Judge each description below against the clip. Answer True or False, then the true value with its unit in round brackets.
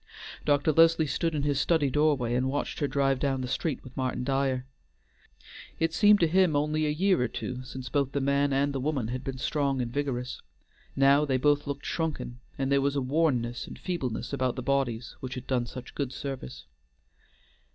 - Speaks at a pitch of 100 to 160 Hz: True (140 Hz)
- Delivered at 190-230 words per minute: True (195 wpm)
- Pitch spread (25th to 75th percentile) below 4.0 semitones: True (2.5 semitones)